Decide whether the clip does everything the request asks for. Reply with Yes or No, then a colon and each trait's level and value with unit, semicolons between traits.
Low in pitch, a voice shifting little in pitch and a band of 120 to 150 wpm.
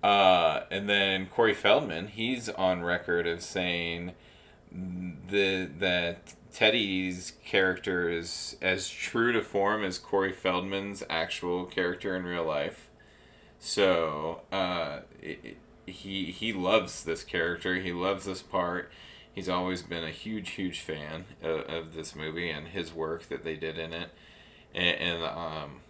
Yes: very low, 90 Hz; narrow, 2.2 semitones; average, 145 wpm